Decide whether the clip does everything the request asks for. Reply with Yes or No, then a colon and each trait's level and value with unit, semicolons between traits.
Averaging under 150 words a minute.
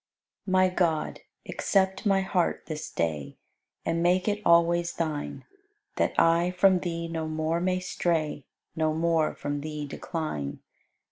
Yes: average, 140 wpm